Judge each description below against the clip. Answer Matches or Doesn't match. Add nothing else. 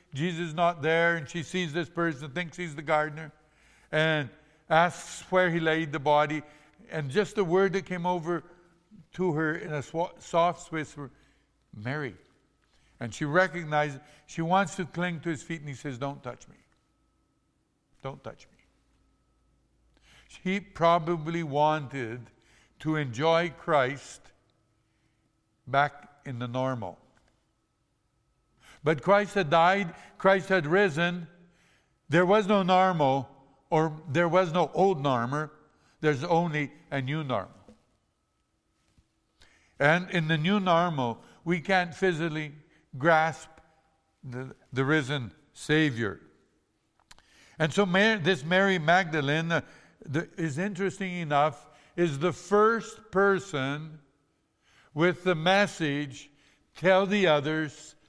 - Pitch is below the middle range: Doesn't match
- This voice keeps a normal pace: Doesn't match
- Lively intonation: Doesn't match